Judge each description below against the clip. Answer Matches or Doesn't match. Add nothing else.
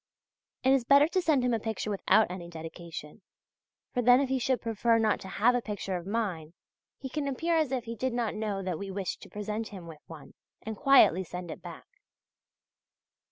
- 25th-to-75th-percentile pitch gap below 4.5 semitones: Doesn't match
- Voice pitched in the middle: Doesn't match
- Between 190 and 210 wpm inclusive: Matches